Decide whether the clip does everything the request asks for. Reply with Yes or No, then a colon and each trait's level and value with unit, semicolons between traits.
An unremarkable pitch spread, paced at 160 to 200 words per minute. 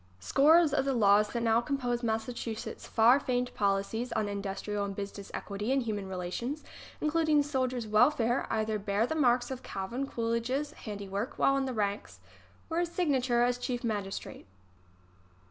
Yes: average, 4.2 semitones; average, 165 wpm